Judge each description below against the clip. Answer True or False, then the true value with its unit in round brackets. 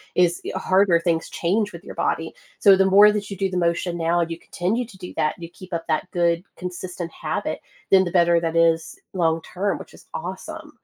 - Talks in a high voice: False (175 Hz)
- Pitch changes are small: True (2.2 semitones)